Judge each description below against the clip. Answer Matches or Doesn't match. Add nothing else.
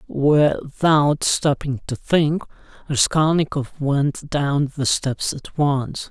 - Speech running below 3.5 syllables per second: Matches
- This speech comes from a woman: Doesn't match